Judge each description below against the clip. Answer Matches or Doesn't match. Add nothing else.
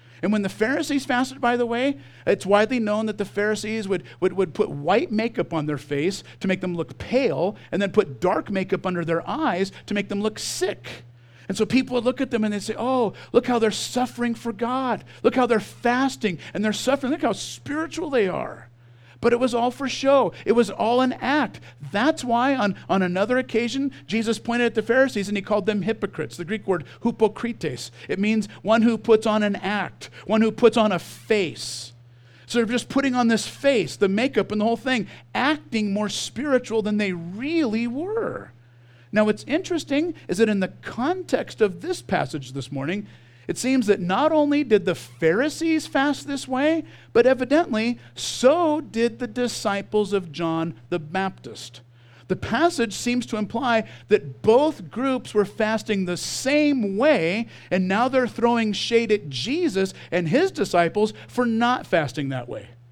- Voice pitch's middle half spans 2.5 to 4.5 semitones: Doesn't match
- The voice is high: Matches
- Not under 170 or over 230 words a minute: Matches